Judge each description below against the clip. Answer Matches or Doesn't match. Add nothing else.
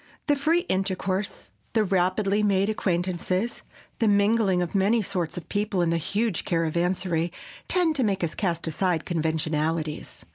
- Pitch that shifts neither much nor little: Matches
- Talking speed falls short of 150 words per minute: Matches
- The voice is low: Doesn't match